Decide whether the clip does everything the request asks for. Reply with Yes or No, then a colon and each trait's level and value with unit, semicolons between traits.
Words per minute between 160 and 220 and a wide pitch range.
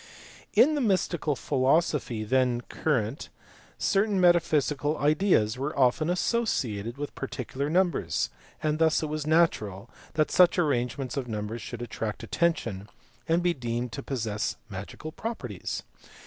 No: slow, 135 wpm; wide, 5.9 semitones